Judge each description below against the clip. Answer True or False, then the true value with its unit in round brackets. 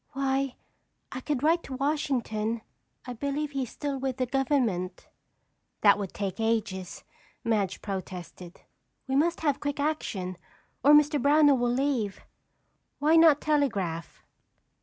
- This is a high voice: True (265 Hz)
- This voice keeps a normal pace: False (130 wpm)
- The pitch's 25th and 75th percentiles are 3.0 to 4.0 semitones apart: False (5.6 semitones)